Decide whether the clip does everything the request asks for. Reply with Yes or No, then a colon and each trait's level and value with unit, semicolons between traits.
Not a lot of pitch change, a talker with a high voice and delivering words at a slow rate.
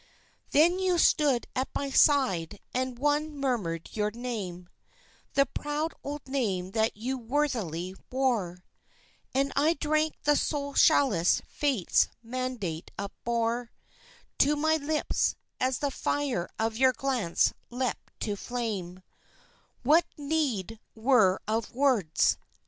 No: wide, 5.4 semitones; very high, 255 Hz; slow, 120 wpm